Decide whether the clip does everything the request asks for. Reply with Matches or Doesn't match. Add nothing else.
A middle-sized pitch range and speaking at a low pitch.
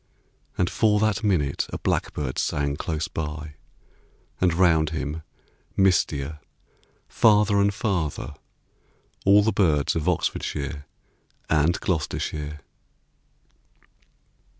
Matches